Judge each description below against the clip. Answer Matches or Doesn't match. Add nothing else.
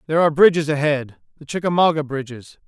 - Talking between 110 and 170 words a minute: Matches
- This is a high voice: Doesn't match